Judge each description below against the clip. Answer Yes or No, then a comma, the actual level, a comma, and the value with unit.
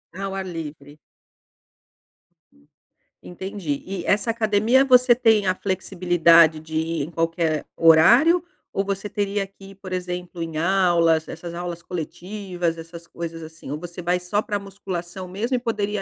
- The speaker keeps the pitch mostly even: No, average, 3.3 semitones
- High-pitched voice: No, medium, 180 Hz